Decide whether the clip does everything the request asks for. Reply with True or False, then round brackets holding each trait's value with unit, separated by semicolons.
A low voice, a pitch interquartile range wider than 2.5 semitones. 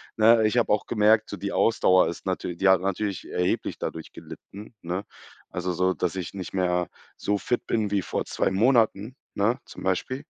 True (100 Hz; 2.9 semitones)